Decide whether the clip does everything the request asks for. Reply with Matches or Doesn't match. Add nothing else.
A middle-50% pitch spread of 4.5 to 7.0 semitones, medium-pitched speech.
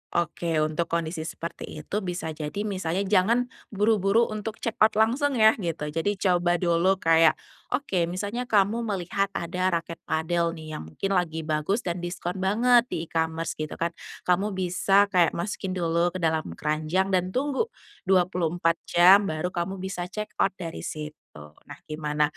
Doesn't match